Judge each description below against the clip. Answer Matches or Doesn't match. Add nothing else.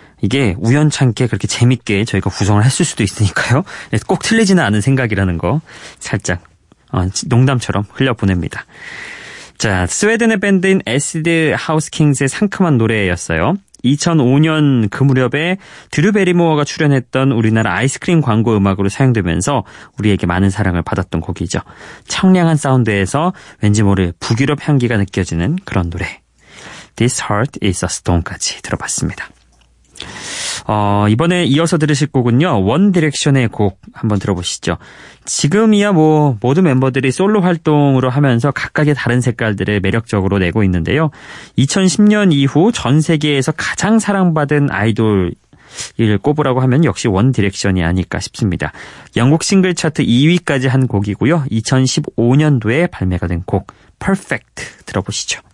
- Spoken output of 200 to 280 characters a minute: Doesn't match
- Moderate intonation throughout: Doesn't match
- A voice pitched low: Matches